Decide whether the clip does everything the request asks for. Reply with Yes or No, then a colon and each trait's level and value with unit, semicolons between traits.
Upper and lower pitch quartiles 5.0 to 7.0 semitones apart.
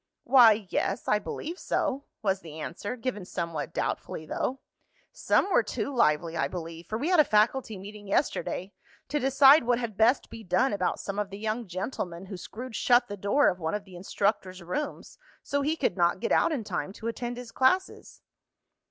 Yes: wide, 5.6 semitones